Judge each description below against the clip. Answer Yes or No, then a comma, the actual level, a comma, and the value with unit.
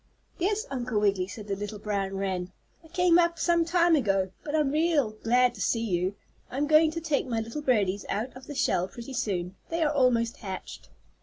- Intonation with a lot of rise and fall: Yes, wide, 7.4 semitones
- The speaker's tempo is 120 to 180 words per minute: No, fast, 205 wpm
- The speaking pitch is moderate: No, high, 240 Hz